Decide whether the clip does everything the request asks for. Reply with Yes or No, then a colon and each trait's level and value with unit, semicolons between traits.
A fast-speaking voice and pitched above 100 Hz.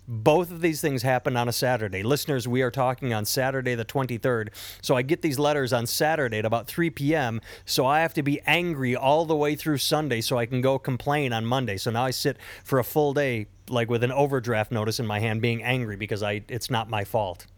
Yes: fast, 235 wpm; low, 125 Hz